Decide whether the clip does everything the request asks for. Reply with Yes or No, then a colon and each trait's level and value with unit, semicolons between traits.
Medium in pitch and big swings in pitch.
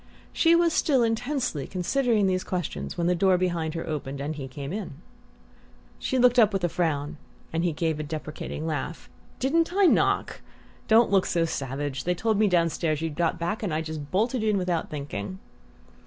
Yes: medium, 175 Hz; wide, 6.0 semitones